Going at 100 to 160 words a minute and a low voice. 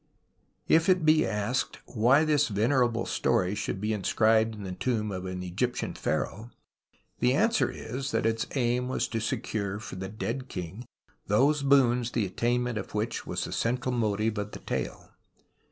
No: average, 170 wpm; low, 115 Hz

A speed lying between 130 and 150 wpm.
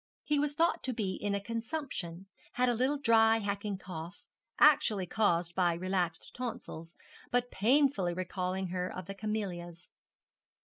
Yes: average, 145 wpm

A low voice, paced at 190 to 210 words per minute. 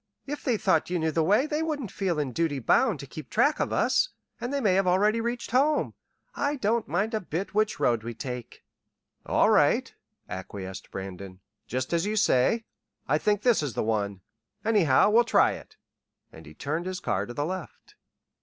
No: medium, 180 Hz; average, 195 wpm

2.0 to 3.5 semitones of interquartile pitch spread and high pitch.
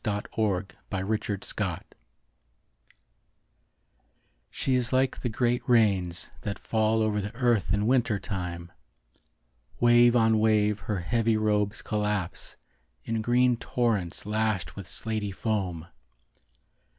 No: narrow, 2.6 semitones; low, 110 Hz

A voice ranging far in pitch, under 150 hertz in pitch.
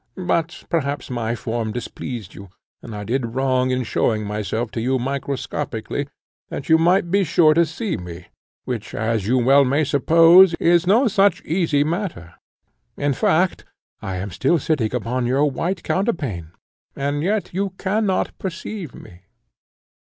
Yes: wide, 6.8 semitones; medium, 140 Hz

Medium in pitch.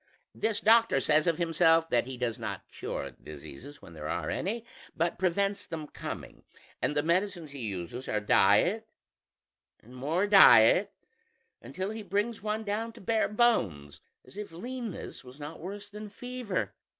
Yes: medium, 175 Hz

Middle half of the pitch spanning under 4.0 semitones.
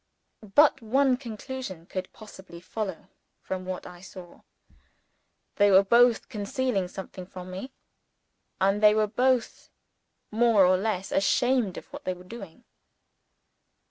No: average, 4.4 semitones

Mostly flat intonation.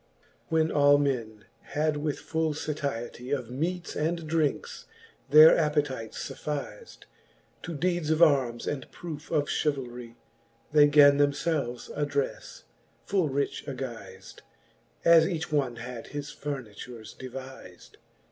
No: average, 3.4 semitones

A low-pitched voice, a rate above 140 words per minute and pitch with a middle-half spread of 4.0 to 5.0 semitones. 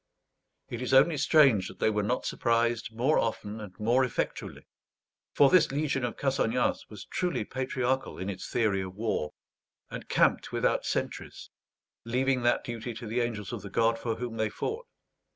No: low, 120 Hz; average, 170 wpm; average, 3.2 semitones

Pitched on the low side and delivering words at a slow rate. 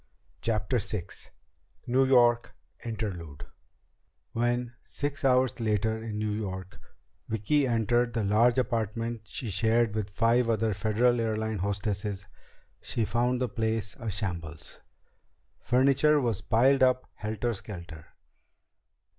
Yes: low, 115 Hz; slow, 115 wpm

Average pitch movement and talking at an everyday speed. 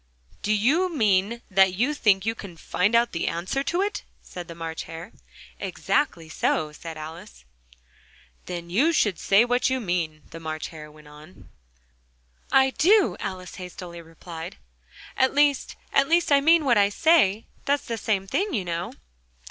No: wide, 8.0 semitones; average, 165 wpm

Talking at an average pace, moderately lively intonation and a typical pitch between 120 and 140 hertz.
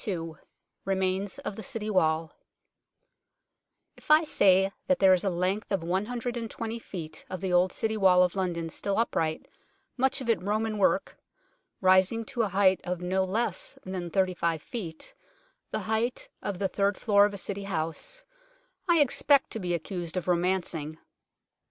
No: average, 160 wpm; average, 3.5 semitones; high, 190 Hz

